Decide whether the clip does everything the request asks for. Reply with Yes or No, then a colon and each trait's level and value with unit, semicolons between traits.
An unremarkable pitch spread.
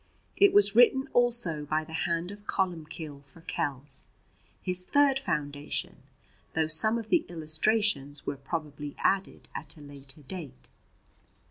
No: wide, 5.9 semitones